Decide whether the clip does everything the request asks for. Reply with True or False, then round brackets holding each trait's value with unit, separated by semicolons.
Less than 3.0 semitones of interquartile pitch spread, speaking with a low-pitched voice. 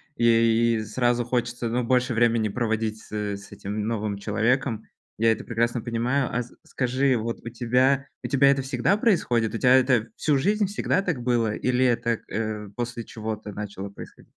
True (2.5 semitones; 120 Hz)